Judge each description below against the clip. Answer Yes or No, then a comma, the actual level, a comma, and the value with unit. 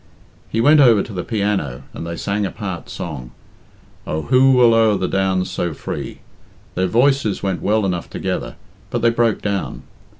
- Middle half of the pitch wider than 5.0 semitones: No, average, 4.4 semitones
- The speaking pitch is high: No, low, 100 Hz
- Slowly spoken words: No, average, 175 wpm